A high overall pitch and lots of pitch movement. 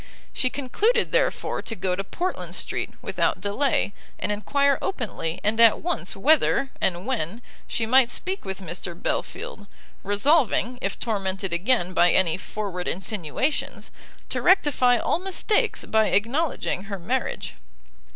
Yes: high, 220 Hz; wide, 6.6 semitones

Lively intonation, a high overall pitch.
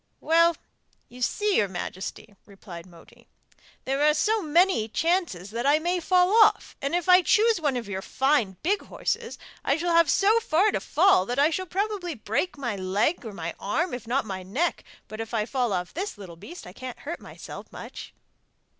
Yes: wide, 9.0 semitones; very high, 280 Hz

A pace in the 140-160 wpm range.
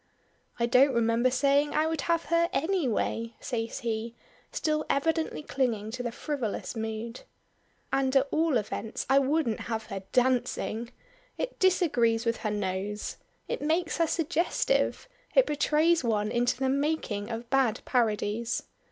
Yes: average, 145 wpm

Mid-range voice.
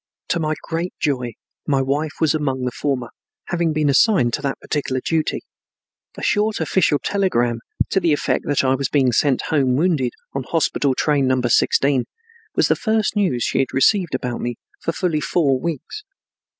Yes: medium, 145 Hz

